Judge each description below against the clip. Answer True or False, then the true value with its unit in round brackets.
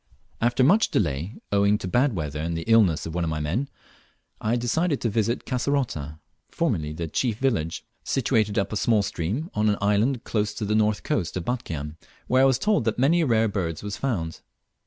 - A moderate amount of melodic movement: False (6.8 semitones)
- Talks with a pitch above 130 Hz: False (105 Hz)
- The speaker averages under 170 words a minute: False (200 wpm)